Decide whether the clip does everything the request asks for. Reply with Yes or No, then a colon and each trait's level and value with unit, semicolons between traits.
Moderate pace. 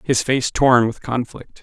Yes: average, 185 wpm